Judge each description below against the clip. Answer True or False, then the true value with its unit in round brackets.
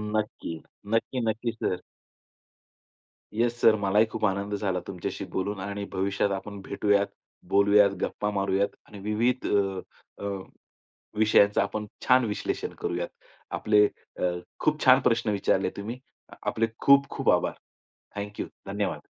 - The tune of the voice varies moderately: False (1.8 semitones)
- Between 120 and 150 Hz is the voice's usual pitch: False (105 Hz)